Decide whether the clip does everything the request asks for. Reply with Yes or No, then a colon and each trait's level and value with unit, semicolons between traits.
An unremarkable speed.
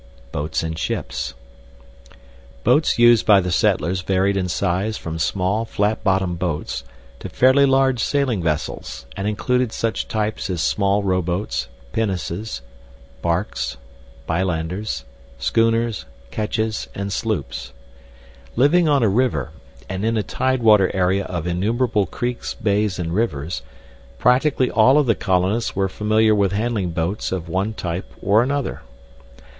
No: slow, 130 wpm